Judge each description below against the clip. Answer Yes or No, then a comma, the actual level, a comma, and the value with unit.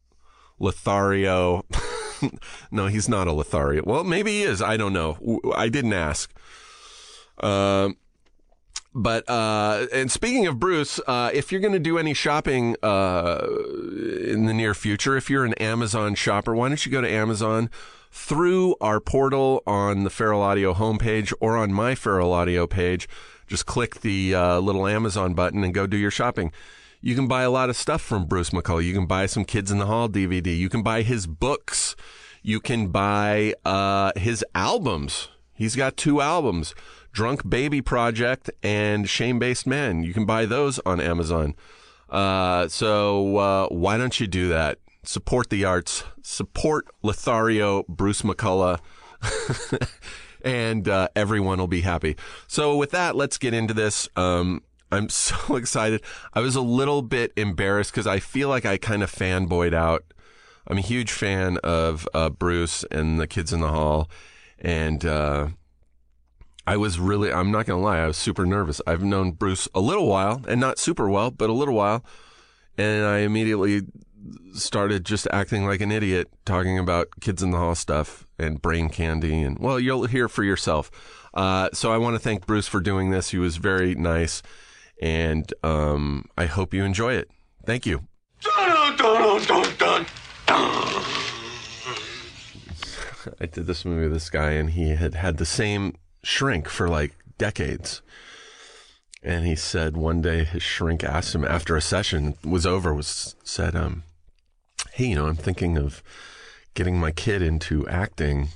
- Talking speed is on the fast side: No, average, 165 wpm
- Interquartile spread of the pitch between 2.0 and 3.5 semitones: No, average, 4.7 semitones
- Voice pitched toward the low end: Yes, low, 100 Hz